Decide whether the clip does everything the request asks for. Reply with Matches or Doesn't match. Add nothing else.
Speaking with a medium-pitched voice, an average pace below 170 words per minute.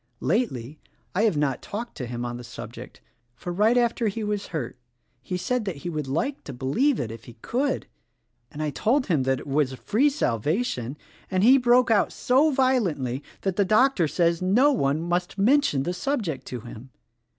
Doesn't match